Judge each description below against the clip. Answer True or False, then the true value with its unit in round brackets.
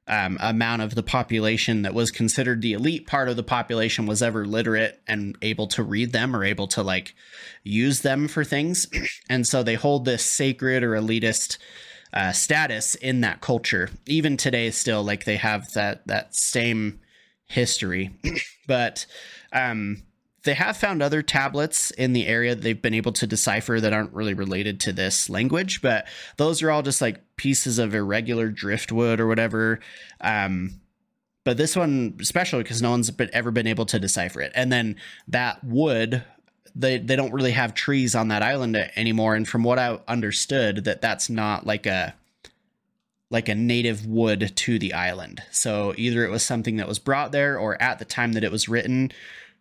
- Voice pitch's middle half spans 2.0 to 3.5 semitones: True (3.1 semitones)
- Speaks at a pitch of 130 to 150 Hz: False (115 Hz)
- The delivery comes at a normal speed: True (185 wpm)